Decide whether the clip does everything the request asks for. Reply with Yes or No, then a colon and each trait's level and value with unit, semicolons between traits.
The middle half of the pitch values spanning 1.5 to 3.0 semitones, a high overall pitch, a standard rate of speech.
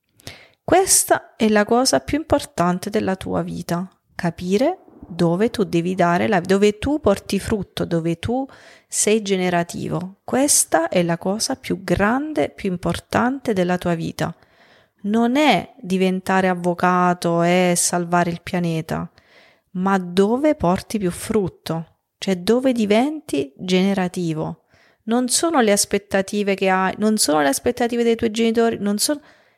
No: average, 4.6 semitones; high, 195 Hz; average, 135 wpm